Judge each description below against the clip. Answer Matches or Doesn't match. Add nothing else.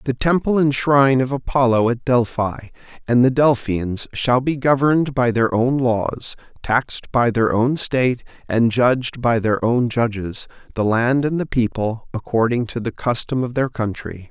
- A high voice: Doesn't match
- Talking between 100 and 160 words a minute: Doesn't match